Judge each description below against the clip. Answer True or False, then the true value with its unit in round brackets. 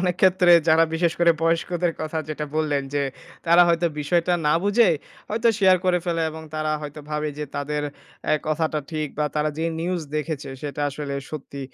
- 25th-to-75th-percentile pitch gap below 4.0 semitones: True (2.5 semitones)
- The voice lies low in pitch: False (160 Hz)